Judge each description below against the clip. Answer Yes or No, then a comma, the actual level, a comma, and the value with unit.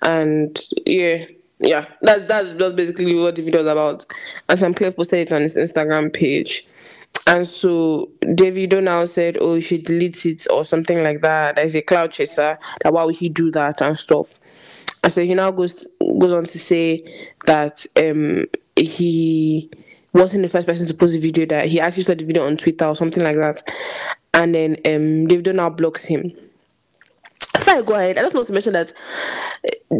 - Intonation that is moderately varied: No, narrow, 2.3 semitones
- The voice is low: No, medium, 170 Hz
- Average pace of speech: Yes, average, 190 wpm